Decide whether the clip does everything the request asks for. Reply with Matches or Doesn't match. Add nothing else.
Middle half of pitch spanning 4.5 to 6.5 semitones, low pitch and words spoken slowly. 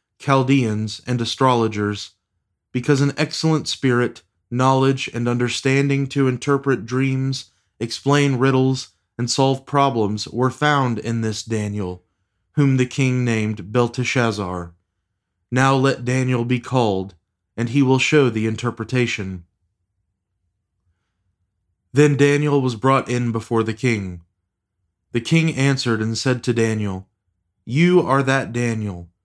Matches